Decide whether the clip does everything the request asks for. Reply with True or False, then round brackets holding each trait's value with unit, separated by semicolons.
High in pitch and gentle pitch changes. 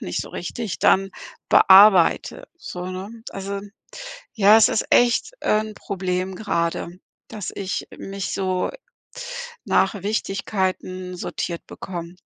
True (195 Hz; 2.3 semitones)